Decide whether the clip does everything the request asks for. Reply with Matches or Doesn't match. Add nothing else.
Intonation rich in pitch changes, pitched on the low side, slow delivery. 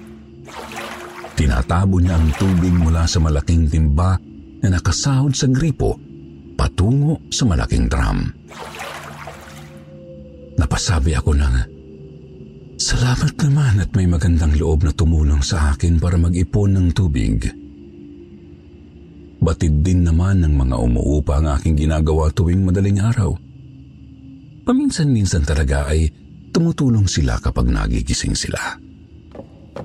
Doesn't match